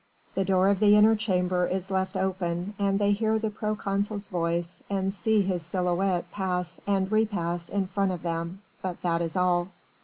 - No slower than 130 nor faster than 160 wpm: No, average, 180 wpm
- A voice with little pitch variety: Yes, narrow, 2.2 semitones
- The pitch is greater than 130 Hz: Yes, high, 190 Hz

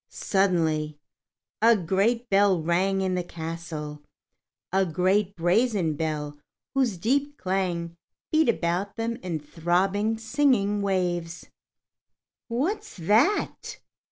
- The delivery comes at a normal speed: No, slow, 100 wpm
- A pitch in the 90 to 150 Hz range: No, high, 190 Hz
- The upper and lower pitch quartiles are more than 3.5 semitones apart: Yes, average, 4.7 semitones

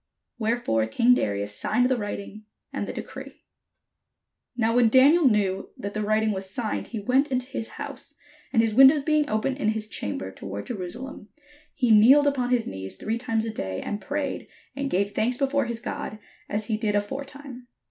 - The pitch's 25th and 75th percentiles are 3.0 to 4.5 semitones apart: Yes, average, 4.1 semitones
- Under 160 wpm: No, average, 180 wpm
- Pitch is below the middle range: No, high, 225 Hz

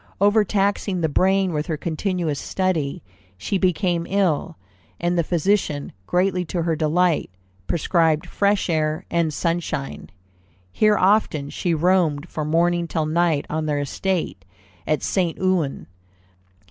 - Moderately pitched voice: Yes, medium, 170 Hz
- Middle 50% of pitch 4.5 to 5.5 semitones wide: No, average, 3.3 semitones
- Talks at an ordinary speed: No, slow, 130 wpm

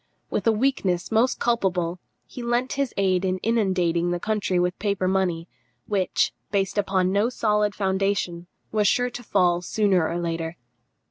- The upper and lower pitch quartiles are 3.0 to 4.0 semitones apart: Yes, average, 3.4 semitones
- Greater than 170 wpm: No, average, 155 wpm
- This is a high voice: Yes, high, 195 Hz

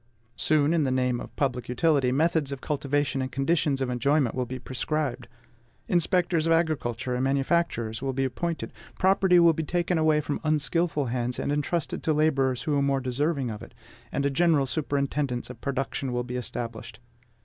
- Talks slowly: No, average, 180 wpm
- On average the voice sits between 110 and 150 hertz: Yes, medium, 140 Hz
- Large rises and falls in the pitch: No, average, 3.7 semitones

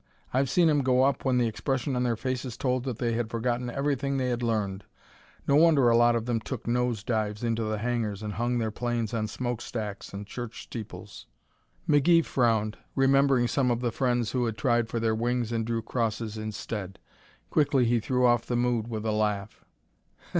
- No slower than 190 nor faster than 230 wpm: Yes, average, 195 wpm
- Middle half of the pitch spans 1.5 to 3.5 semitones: Yes, narrow, 2.4 semitones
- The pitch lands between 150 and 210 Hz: No, low, 120 Hz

